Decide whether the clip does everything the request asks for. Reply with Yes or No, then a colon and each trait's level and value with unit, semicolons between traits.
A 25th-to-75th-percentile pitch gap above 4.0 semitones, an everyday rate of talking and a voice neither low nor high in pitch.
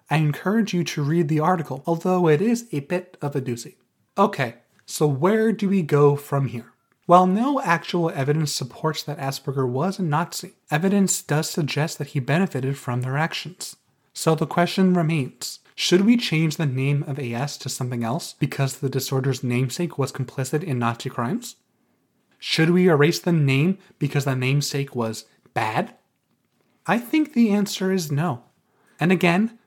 Yes: average, 5.0 semitones; average, 170 wpm; medium, 155 Hz